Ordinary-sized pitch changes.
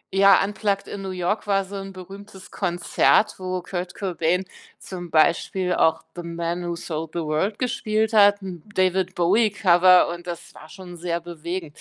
No: narrow, 2.3 semitones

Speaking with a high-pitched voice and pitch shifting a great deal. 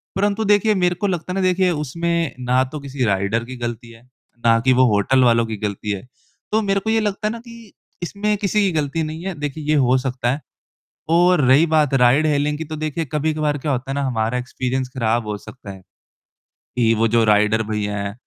No: medium, 140 Hz; wide, 6.9 semitones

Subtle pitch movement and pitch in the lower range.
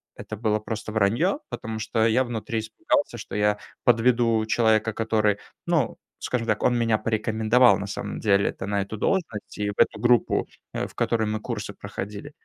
Yes: narrow, 1.9 semitones; low, 110 Hz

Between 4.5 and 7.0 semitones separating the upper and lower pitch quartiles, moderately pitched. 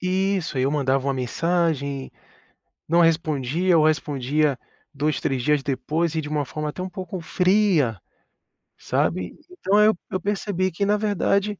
Yes: average, 5.0 semitones; medium, 160 Hz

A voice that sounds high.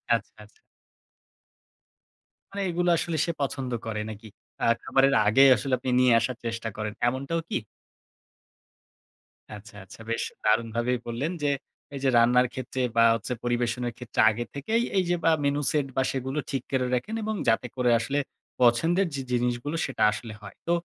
No: low, 125 Hz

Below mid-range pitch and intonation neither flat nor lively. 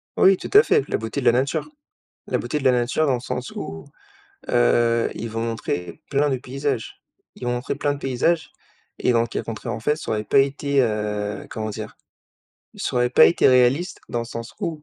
Yes: low, 125 Hz; average, 3.9 semitones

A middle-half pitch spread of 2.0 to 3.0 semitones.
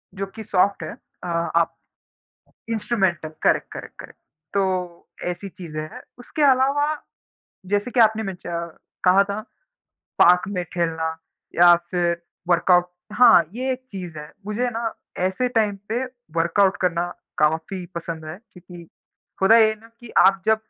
No: average, 4.3 semitones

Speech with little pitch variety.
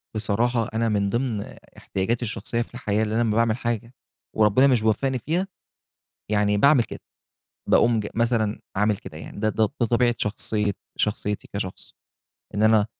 Yes: narrow, 2.2 semitones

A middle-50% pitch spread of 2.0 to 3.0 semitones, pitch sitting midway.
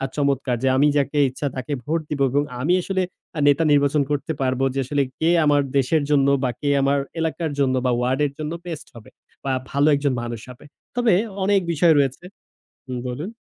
Yes: narrow, 2.6 semitones; medium, 145 Hz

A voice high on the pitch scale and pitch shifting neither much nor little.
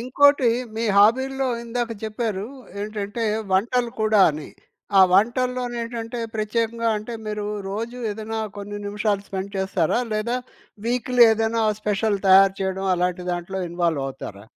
Yes: high, 215 Hz; average, 3.4 semitones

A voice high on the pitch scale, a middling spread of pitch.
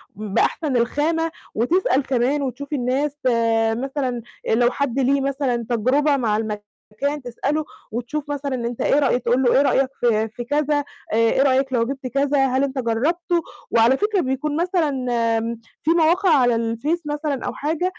Yes: very high, 270 Hz; average, 3.6 semitones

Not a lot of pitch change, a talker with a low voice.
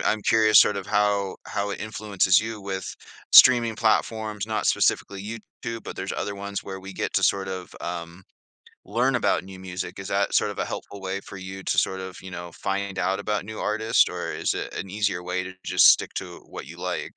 Yes: narrow, 2.2 semitones; low, 100 Hz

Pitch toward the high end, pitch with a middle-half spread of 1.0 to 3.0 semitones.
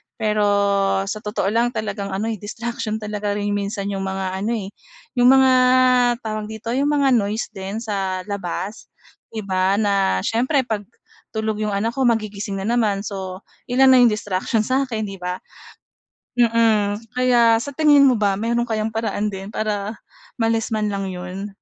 Yes: high, 215 Hz; narrow, 2.5 semitones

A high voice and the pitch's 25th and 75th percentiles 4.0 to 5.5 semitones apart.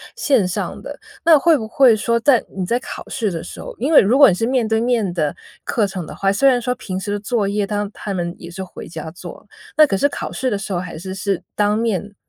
Yes: high, 205 Hz; average, 4.4 semitones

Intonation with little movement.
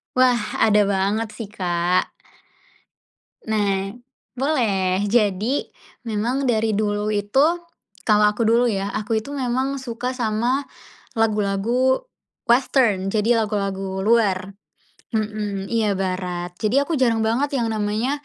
No: average, 3.3 semitones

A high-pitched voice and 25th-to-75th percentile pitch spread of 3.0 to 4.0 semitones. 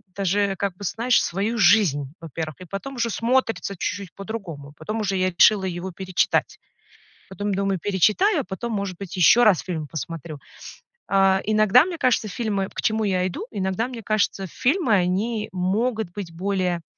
Yes: high, 195 Hz; average, 3.3 semitones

